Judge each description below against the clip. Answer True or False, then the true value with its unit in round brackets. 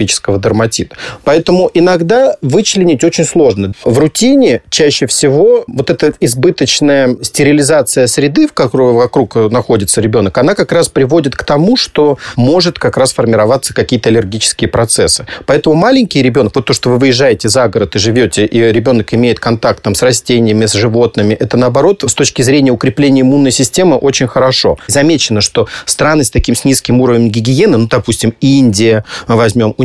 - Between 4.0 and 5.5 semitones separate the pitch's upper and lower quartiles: True (4.4 semitones)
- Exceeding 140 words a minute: True (160 wpm)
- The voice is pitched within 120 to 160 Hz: True (130 Hz)